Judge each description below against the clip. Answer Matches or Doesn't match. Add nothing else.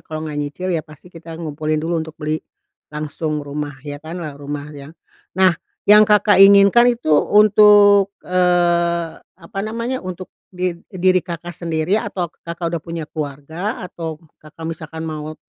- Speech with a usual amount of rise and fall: Matches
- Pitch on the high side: Doesn't match